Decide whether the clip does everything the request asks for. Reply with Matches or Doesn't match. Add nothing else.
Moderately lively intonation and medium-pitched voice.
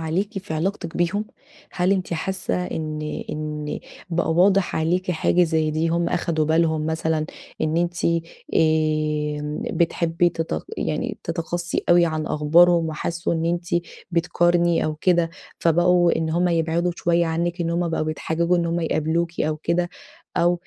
Doesn't match